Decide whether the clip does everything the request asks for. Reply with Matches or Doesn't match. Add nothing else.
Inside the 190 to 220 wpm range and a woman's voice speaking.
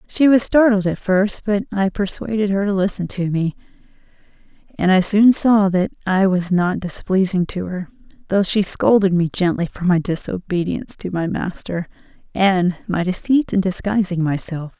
Doesn't match